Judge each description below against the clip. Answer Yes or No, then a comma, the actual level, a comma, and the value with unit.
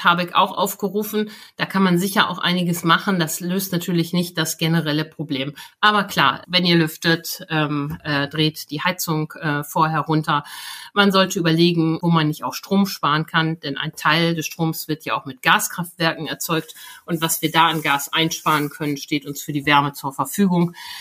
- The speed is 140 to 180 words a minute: No, fast, 190 wpm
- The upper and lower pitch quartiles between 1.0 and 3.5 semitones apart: Yes, average, 2.7 semitones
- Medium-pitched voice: Yes, medium, 165 Hz